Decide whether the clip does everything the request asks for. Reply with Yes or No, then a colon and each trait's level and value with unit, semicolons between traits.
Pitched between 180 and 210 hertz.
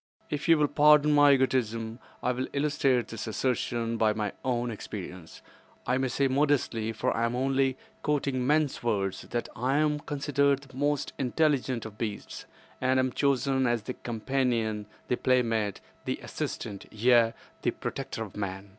No: low, 125 Hz